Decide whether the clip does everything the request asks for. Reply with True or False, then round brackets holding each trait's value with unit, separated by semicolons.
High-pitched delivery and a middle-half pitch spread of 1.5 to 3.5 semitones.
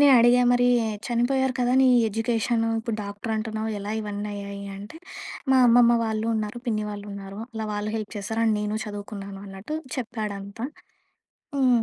True (220 Hz; 2.7 semitones)